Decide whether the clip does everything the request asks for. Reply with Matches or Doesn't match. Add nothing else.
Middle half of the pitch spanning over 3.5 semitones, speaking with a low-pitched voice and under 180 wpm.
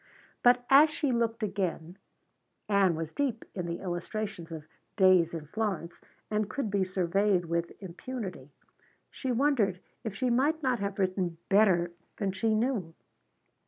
Doesn't match